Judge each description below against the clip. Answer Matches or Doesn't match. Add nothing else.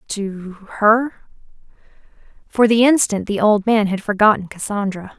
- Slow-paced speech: Matches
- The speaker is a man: Doesn't match